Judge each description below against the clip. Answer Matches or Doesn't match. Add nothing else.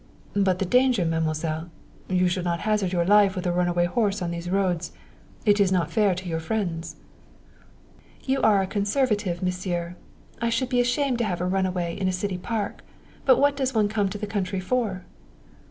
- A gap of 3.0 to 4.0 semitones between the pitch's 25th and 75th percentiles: Matches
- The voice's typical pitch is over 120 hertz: Matches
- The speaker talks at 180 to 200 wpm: Matches